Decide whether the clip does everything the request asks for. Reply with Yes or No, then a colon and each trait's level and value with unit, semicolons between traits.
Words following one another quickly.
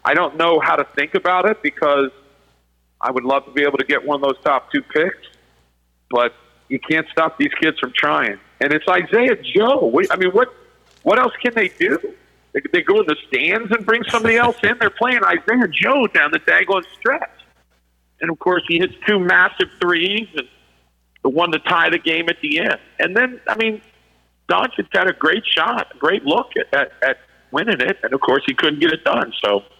Yes: fast, 215 wpm